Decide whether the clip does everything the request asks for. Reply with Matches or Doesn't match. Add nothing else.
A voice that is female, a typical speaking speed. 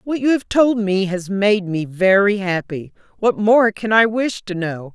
Matches